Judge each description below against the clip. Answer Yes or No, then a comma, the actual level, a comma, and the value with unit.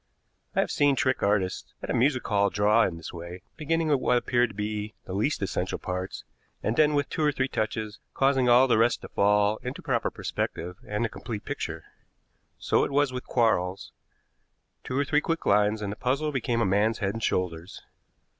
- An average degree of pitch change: Yes, average, 4.8 semitones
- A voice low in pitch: Yes, low, 110 Hz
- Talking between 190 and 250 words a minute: Yes, average, 200 wpm